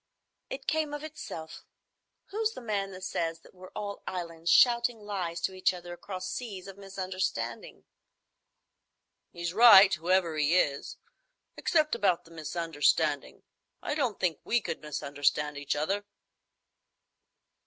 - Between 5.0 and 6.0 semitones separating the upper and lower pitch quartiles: No, average, 4.5 semitones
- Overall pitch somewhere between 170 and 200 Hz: Yes, medium, 185 Hz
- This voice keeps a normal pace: No, slow, 130 wpm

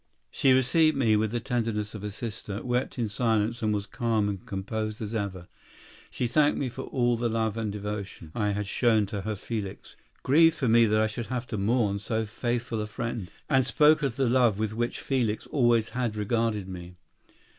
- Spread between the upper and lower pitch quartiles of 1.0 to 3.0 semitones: Yes, narrow, 2.6 semitones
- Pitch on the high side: No, low, 110 Hz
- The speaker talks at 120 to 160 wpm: No, average, 200 wpm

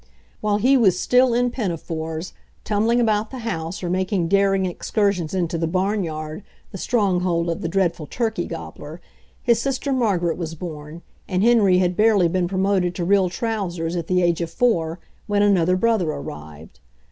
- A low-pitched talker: No, medium, 185 Hz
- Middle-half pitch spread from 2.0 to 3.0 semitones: No, average, 4.1 semitones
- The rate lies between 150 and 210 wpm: Yes, average, 170 wpm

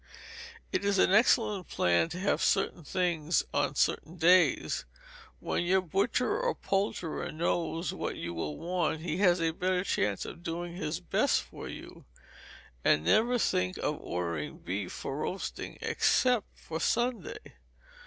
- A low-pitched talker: No, medium, 175 Hz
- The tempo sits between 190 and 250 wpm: No, average, 145 wpm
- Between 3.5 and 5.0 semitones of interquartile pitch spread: Yes, average, 3.8 semitones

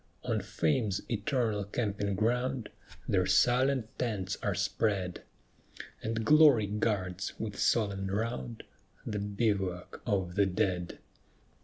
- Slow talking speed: Yes, slow, 110 wpm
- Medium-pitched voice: No, low, 105 Hz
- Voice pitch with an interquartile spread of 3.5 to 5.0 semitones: No, average, 3.1 semitones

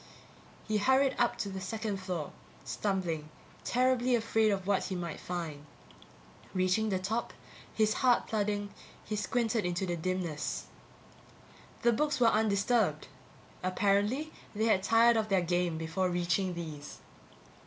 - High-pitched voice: Yes, high, 200 Hz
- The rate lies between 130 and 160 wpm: Yes, slow, 135 wpm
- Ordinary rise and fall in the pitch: Yes, average, 3.9 semitones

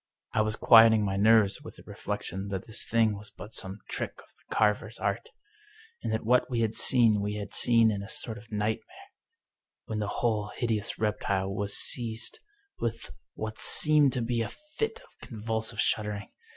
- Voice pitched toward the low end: Yes, low, 110 Hz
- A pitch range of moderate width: No, narrow, 1.8 semitones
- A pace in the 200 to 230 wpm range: No, average, 185 wpm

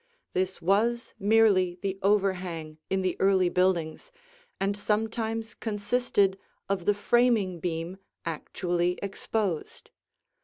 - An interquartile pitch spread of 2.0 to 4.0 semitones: Yes, average, 2.8 semitones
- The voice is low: No, high, 195 Hz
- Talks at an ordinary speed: No, slow, 105 wpm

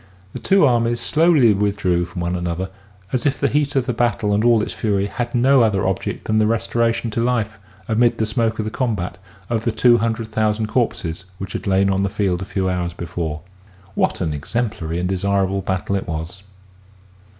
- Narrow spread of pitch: No, average, 3.8 semitones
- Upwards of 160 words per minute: Yes, average, 200 wpm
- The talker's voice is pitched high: No, low, 105 Hz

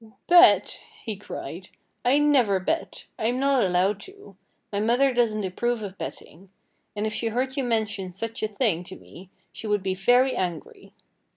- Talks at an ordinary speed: Yes, average, 170 wpm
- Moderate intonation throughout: Yes, average, 4.7 semitones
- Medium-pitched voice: No, high, 220 Hz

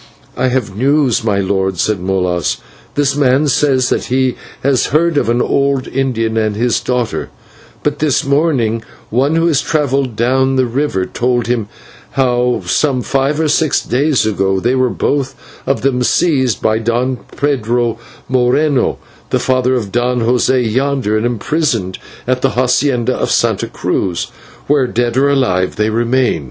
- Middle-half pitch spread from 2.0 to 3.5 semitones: Yes, average, 3.2 semitones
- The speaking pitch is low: Yes, low, 125 Hz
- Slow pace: No, average, 165 wpm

